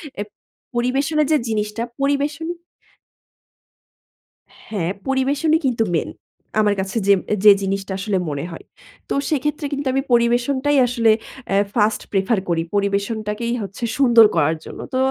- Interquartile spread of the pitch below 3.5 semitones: No, average, 5.3 semitones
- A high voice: Yes, high, 230 Hz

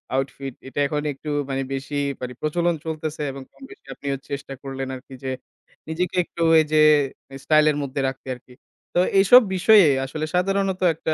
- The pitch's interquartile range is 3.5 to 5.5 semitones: Yes, average, 4.2 semitones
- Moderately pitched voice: Yes, medium, 150 Hz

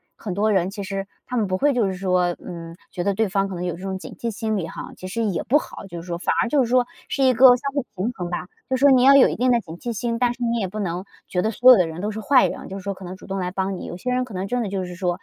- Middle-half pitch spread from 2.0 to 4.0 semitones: No, average, 4.7 semitones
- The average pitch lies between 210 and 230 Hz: No, high, 195 Hz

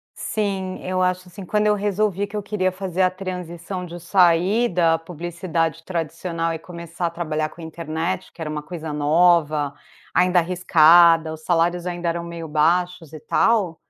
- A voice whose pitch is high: No, medium, 175 Hz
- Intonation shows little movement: Yes, narrow, 2.0 semitones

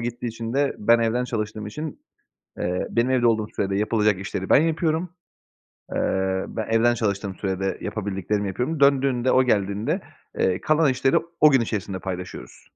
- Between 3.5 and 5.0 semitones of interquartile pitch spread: Yes, average, 4.5 semitones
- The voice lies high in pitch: No, low, 115 Hz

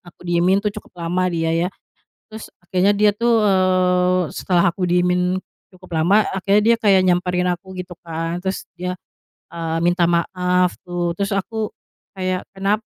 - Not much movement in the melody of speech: Yes, narrow, 1.7 semitones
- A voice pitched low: No, medium, 180 Hz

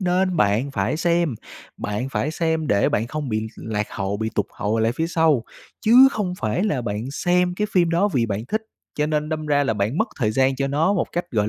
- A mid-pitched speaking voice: Yes, medium, 145 Hz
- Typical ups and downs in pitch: No, wide, 7.7 semitones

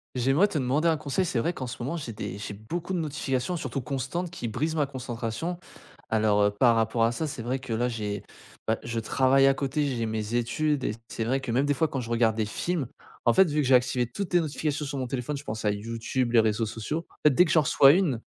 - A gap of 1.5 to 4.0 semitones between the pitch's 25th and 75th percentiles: No, average, 4.7 semitones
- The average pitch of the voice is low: Yes, low, 130 Hz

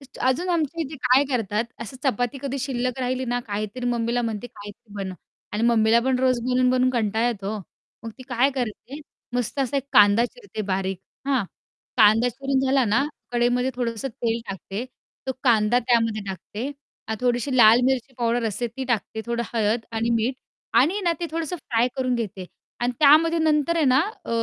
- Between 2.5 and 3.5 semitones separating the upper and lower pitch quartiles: Yes, average, 2.9 semitones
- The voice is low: No, high, 245 Hz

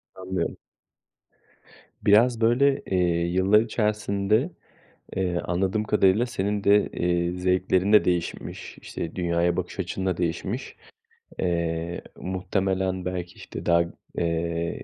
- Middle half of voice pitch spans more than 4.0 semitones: No, average, 2.9 semitones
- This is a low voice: Yes, very low, 95 Hz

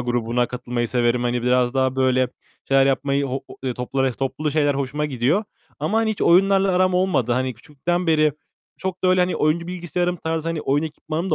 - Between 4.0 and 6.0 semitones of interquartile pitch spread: Yes, wide, 5.5 semitones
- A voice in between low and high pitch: Yes, medium, 145 Hz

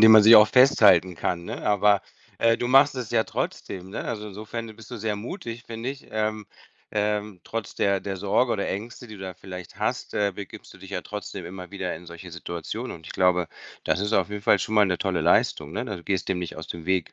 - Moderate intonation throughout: Yes, average, 3.4 semitones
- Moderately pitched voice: No, low, 100 Hz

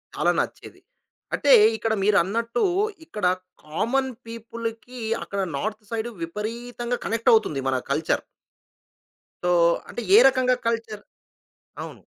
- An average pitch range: No, narrow, 2.3 semitones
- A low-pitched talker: No, high, 225 Hz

